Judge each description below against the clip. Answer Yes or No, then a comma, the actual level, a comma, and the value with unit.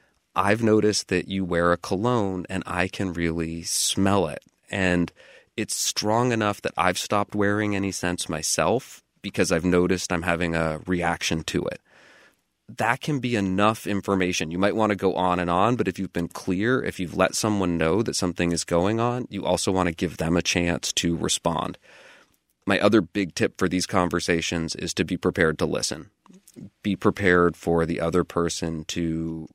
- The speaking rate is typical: Yes, average, 185 wpm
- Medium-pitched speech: No, very low, 90 Hz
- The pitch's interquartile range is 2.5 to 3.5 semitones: Yes, average, 2.9 semitones